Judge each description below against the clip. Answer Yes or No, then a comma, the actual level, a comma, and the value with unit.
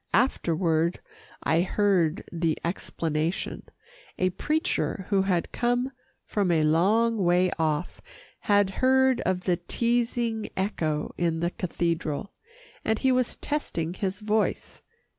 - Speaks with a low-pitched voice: No, medium, 185 Hz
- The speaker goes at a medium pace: No, slow, 120 wpm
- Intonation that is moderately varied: Yes, average, 4.9 semitones